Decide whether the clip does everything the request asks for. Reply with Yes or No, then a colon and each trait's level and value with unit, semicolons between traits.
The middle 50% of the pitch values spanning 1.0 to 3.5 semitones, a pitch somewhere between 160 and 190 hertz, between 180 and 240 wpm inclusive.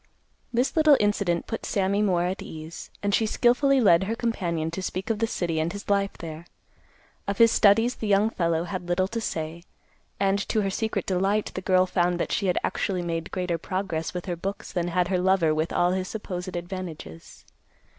Yes: average, 3.0 semitones; medium, 185 Hz; average, 200 wpm